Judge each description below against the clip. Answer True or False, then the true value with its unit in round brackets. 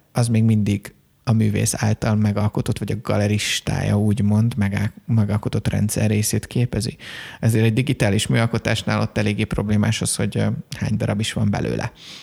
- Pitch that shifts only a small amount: True (1.6 semitones)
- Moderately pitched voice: False (110 Hz)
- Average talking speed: True (140 wpm)